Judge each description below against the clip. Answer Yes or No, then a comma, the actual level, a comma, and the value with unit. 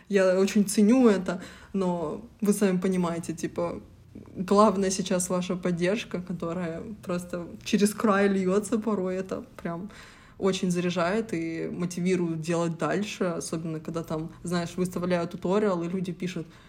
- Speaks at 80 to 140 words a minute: Yes, average, 130 wpm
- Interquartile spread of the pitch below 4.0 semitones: Yes, average, 2.7 semitones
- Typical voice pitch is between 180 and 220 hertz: Yes, medium, 185 Hz